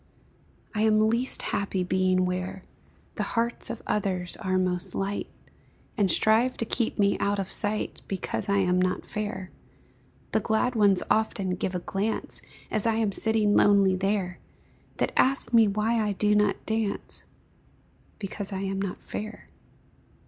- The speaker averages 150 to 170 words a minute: Yes, average, 155 wpm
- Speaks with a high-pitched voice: Yes, high, 200 Hz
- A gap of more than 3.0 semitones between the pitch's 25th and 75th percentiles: No, narrow, 2.5 semitones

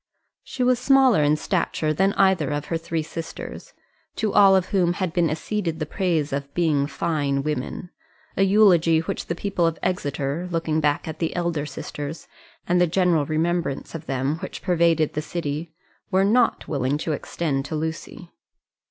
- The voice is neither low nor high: Yes, medium, 165 Hz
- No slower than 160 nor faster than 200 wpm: Yes, average, 170 wpm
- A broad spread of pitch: No, average, 3.2 semitones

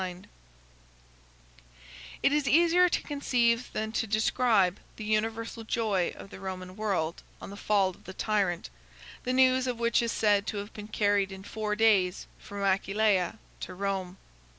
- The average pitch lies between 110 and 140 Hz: No, high, 210 Hz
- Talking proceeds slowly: No, average, 160 wpm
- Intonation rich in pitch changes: No, average, 2.9 semitones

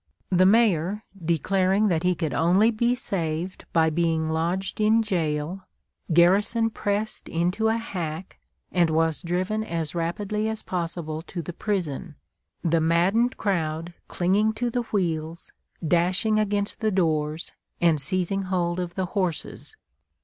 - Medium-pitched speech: Yes, medium, 180 Hz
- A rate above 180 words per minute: No, slow, 135 wpm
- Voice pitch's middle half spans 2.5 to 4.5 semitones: Yes, average, 3.9 semitones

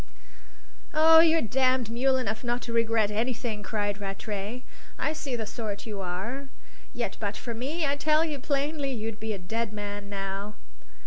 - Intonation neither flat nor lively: Yes, average, 4.7 semitones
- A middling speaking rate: Yes, average, 170 wpm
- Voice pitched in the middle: No, high, 230 Hz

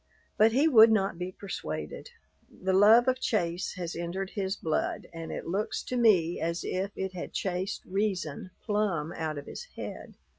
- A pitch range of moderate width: Yes, average, 3.9 semitones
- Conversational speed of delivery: Yes, average, 175 wpm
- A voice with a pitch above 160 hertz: Yes, high, 190 Hz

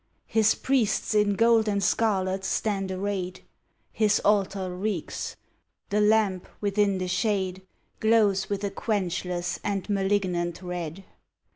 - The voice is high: Yes, high, 200 Hz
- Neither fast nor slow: No, slow, 120 wpm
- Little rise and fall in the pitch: Yes, narrow, 2.2 semitones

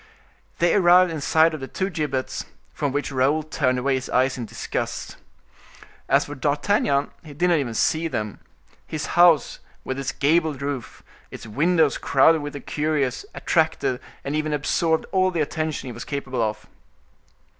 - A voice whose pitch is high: No, medium, 145 Hz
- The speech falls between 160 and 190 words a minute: Yes, average, 165 wpm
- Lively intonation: No, average, 3.2 semitones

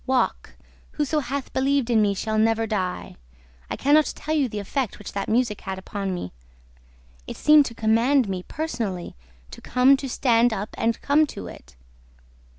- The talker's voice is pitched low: No, high, 230 Hz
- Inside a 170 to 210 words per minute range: Yes, average, 180 wpm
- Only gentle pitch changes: No, average, 5.3 semitones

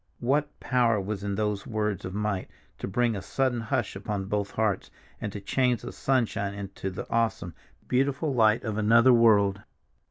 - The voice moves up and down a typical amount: Yes, average, 3.3 semitones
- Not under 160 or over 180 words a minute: Yes, average, 170 wpm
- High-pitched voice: No, low, 110 Hz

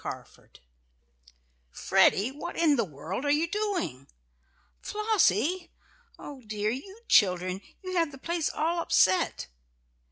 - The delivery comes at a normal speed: No, slow, 120 wpm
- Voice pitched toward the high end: Yes, very high, 285 Hz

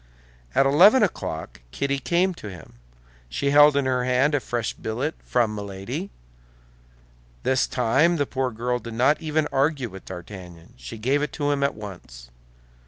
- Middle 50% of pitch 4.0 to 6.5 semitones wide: Yes, wide, 5.4 semitones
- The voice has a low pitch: Yes, low, 130 Hz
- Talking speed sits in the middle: Yes, average, 165 wpm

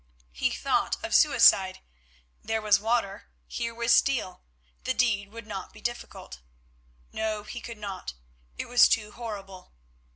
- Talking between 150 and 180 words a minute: No, average, 140 wpm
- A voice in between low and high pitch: No, high, 220 Hz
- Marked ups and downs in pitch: No, average, 2.8 semitones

